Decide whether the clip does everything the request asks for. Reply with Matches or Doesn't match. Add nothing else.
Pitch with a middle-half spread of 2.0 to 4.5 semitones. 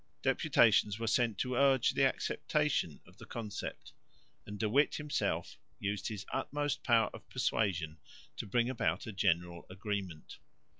Doesn't match